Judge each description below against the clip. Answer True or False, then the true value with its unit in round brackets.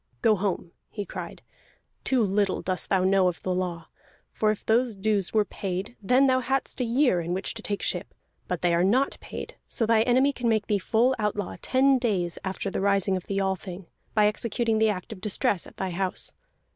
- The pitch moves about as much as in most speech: True (3.6 semitones)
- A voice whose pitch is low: False (205 Hz)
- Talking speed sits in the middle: False (210 wpm)